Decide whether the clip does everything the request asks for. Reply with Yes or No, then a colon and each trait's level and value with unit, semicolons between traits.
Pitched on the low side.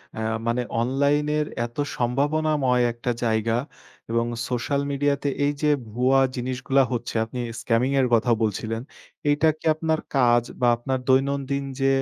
Yes: low, 130 Hz